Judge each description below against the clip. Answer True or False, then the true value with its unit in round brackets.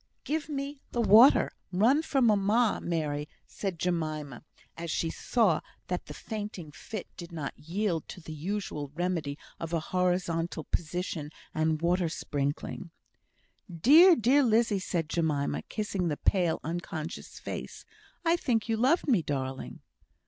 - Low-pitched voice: False (180 Hz)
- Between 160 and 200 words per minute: False (140 wpm)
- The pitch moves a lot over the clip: True (5.7 semitones)